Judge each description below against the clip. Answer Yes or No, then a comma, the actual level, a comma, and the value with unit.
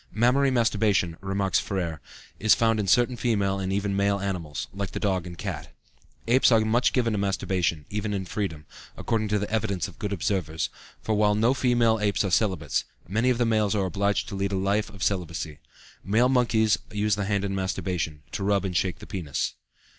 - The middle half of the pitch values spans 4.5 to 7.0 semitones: No, narrow, 2.5 semitones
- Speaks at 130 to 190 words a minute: No, average, 200 wpm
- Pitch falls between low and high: No, low, 100 Hz